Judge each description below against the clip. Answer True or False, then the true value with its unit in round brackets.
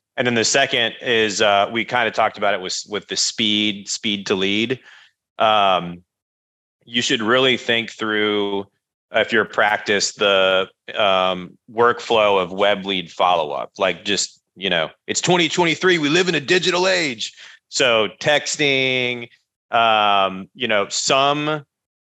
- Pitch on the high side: False (110 Hz)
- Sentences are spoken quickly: False (145 wpm)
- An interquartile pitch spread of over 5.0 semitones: True (5.5 semitones)